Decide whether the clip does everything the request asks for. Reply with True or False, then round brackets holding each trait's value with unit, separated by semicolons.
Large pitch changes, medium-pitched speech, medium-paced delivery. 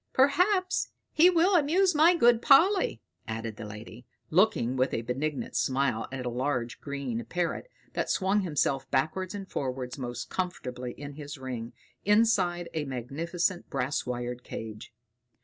True (8.8 semitones; 145 Hz; 145 wpm)